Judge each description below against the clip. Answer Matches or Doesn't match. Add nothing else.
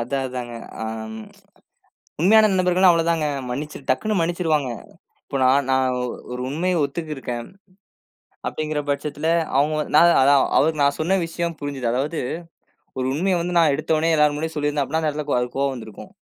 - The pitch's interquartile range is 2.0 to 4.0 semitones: Matches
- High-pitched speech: Doesn't match